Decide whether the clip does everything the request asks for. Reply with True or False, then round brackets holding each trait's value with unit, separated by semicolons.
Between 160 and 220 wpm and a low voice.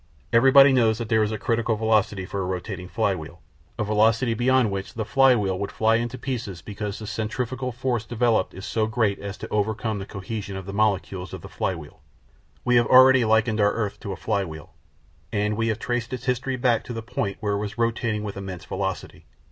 True (205 wpm; 110 Hz)